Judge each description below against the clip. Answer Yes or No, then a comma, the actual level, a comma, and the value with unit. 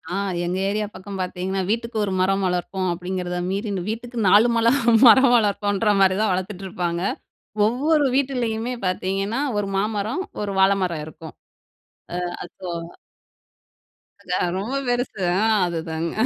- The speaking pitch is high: Yes, high, 195 Hz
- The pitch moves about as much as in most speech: Yes, average, 3.6 semitones